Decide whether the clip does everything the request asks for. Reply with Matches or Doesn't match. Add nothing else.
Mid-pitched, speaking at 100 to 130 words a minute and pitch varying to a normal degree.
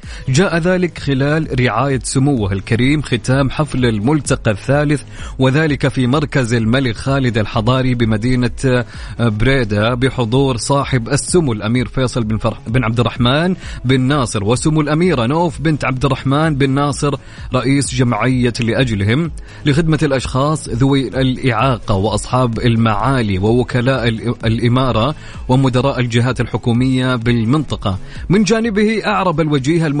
Doesn't match